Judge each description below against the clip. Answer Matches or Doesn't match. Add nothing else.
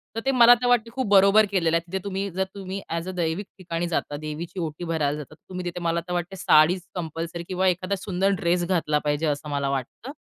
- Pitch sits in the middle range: Matches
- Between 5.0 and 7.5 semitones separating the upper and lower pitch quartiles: Doesn't match